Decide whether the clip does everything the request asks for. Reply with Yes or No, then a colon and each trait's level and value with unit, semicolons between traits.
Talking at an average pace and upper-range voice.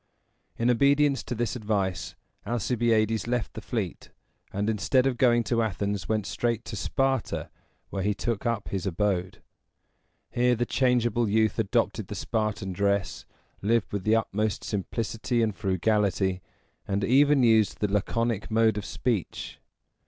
No: average, 145 wpm; low, 110 Hz